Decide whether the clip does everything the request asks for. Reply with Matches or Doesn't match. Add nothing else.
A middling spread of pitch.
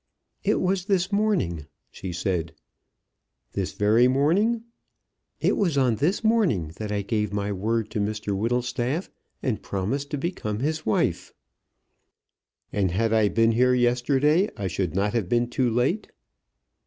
Doesn't match